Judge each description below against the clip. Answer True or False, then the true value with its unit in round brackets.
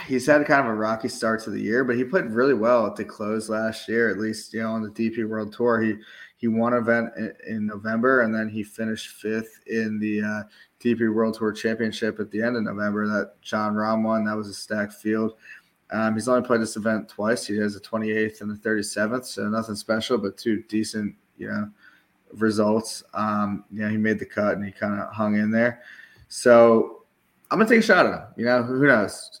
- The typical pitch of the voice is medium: False (110 Hz)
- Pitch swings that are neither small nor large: False (1.1 semitones)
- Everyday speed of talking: False (230 wpm)